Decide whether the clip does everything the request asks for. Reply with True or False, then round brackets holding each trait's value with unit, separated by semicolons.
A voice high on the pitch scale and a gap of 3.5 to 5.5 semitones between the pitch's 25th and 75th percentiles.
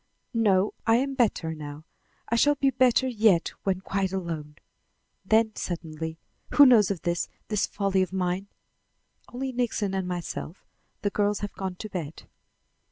True (195 Hz; 4.3 semitones)